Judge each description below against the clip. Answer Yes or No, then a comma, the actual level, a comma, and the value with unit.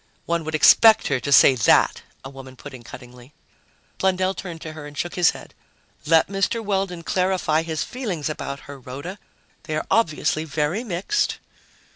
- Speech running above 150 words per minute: Yes, average, 170 wpm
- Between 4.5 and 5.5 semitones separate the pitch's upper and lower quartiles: Yes, average, 4.9 semitones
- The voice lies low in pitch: No, medium, 160 Hz